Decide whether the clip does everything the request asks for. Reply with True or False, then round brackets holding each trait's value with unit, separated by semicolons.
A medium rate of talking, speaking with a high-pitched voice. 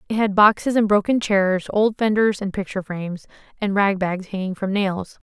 True (195 wpm; 200 Hz)